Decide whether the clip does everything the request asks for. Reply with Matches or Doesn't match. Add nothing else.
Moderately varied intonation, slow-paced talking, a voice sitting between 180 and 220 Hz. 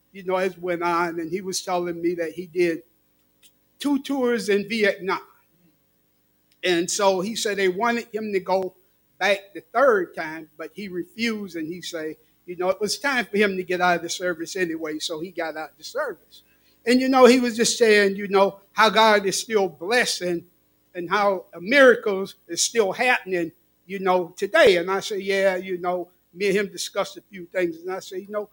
Doesn't match